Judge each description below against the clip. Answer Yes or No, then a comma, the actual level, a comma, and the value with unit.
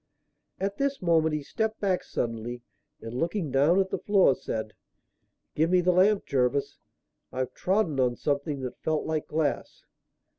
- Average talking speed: Yes, average, 155 wpm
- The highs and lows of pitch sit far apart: Yes, wide, 6.4 semitones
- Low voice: No, medium, 155 Hz